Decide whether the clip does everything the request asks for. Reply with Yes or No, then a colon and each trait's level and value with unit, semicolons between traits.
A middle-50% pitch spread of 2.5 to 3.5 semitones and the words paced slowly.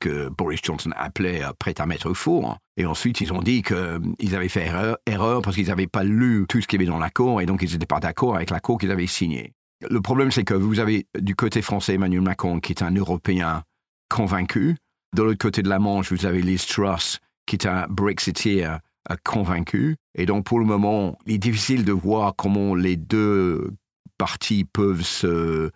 No: average, 3.0 semitones; average, 205 wpm